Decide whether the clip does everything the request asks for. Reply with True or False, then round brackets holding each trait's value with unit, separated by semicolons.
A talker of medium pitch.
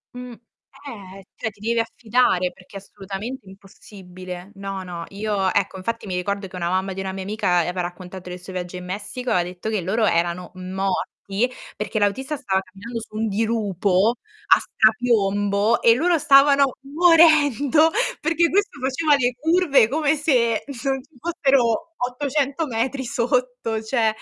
False (220 Hz)